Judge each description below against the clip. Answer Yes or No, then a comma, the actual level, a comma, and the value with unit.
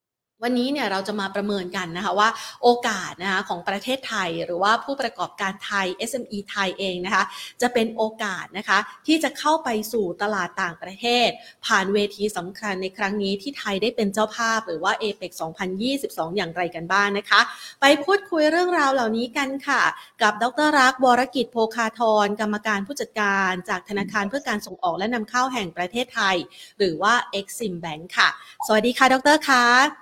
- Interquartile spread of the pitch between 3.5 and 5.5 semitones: Yes, average, 3.9 semitones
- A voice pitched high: Yes, high, 215 Hz